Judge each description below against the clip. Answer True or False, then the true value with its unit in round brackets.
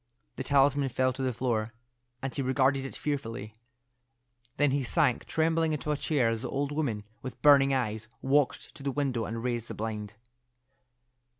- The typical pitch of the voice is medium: False (130 Hz)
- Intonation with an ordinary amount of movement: True (3.5 semitones)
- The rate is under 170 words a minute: False (175 wpm)